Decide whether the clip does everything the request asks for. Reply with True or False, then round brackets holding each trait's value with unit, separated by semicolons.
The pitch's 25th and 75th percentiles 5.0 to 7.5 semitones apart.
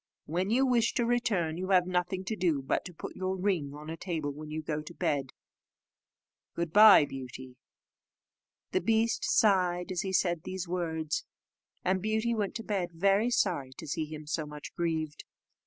False (4.2 semitones)